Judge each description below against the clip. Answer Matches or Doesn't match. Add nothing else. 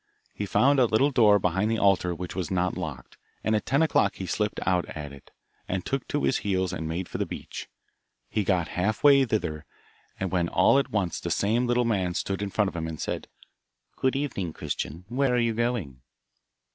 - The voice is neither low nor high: Doesn't match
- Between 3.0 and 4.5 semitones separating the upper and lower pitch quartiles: Doesn't match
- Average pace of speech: Doesn't match